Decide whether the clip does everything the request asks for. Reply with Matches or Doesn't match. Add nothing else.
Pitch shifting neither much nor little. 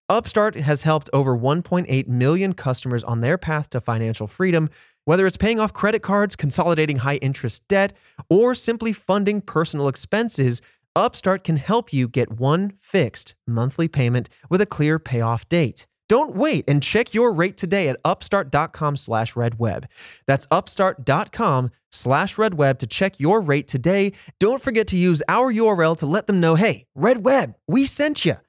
Doesn't match